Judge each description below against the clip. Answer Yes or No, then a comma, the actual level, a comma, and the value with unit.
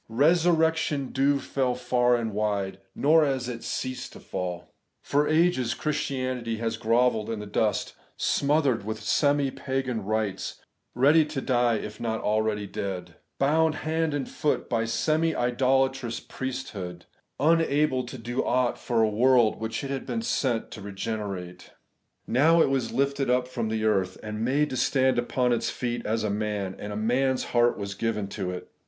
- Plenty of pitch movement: No, average, 4.1 semitones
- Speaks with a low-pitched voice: Yes, low, 120 Hz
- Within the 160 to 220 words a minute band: Yes, average, 175 wpm